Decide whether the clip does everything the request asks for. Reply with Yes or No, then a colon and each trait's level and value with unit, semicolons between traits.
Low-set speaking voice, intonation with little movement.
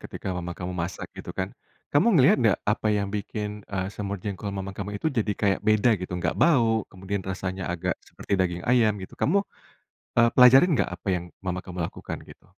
No: low, 100 Hz; average, 3.3 semitones